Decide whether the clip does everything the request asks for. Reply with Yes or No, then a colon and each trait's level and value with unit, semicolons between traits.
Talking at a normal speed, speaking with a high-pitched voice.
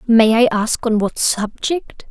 Yes: average, 170 wpm; high, 230 Hz